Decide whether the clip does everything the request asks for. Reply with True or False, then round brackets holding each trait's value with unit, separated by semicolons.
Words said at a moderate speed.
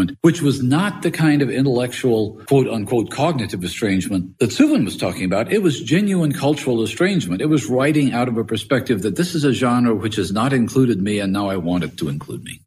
False (220 wpm)